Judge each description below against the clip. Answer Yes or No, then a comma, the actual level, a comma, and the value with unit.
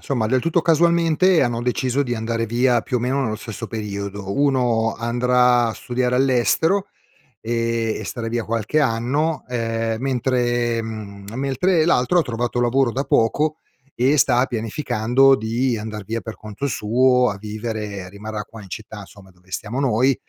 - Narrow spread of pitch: No, average, 3.0 semitones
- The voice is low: Yes, low, 120 Hz